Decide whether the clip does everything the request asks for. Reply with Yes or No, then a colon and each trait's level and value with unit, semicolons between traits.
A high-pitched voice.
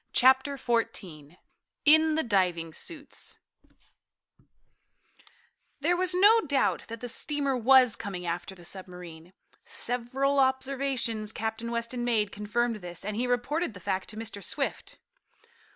Yes: high, 235 Hz